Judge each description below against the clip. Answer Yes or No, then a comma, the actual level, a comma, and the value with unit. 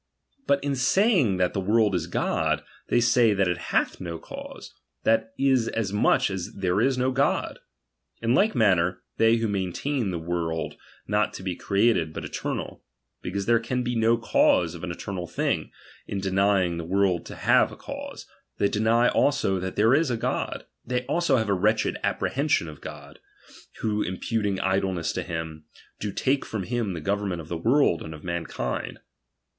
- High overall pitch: No, low, 100 Hz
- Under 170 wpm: No, average, 185 wpm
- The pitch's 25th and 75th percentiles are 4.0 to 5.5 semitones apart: Yes, average, 4.8 semitones